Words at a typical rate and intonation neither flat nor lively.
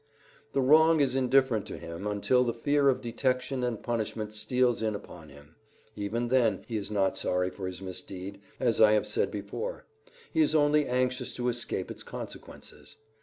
Yes: average, 175 wpm; average, 4.2 semitones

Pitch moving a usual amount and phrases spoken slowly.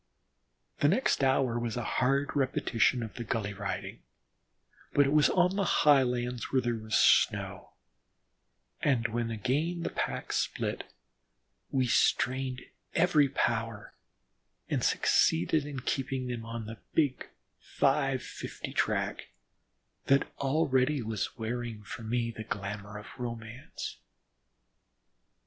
Yes: average, 3.2 semitones; slow, 125 wpm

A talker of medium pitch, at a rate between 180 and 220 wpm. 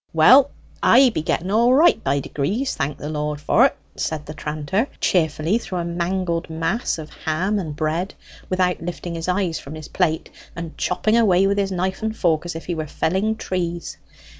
Yes: medium, 175 Hz; average, 190 wpm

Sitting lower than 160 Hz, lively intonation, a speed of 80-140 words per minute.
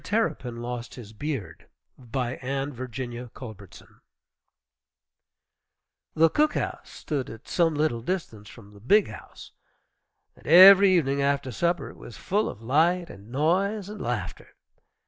Yes: low, 135 Hz; wide, 6.5 semitones; slow, 135 wpm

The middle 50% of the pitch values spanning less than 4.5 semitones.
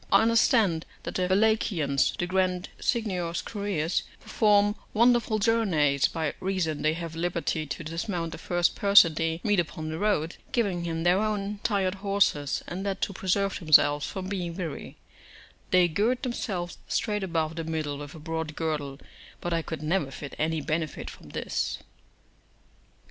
Yes: average, 4.0 semitones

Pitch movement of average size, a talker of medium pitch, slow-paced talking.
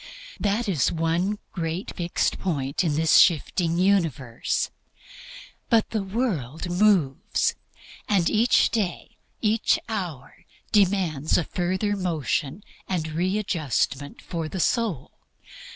Yes: average, 4.3 semitones; medium, 175 Hz; slow, 105 wpm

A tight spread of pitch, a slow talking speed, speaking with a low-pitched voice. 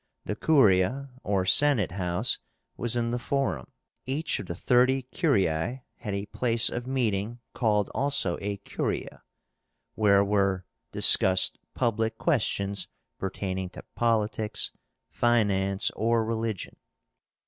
No: average, 3.8 semitones; slow, 115 wpm; low, 110 Hz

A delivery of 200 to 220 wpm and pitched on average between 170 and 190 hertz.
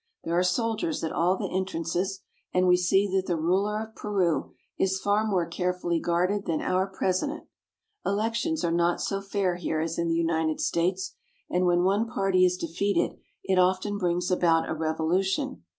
No: average, 180 wpm; medium, 185 Hz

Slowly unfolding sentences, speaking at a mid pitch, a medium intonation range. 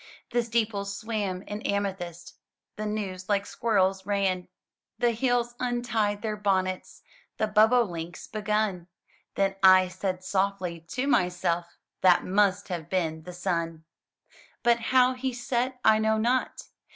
No: slow, 130 wpm; high, 200 Hz; average, 3.5 semitones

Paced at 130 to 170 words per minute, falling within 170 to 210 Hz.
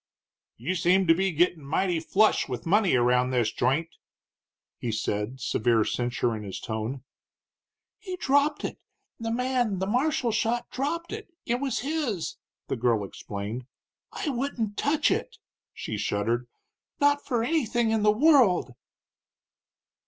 Yes: average, 140 wpm; high, 190 Hz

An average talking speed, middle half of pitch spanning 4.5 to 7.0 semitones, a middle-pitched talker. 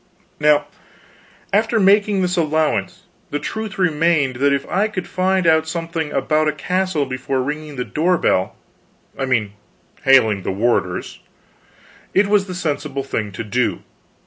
Yes: average, 145 wpm; wide, 5.6 semitones; medium, 155 Hz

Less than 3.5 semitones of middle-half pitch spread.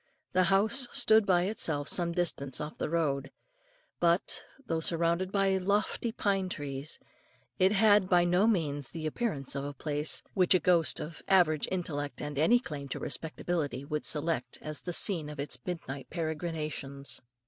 No: average, 4.2 semitones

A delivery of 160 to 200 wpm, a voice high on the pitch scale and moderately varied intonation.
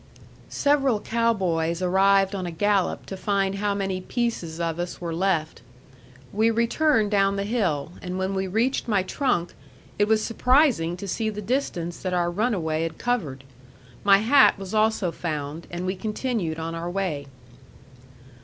Yes: average, 165 wpm; high, 195 Hz; average, 4.2 semitones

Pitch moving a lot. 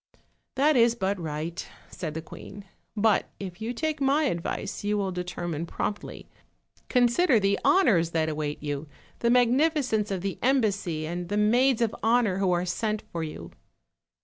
Yes: wide, 5.8 semitones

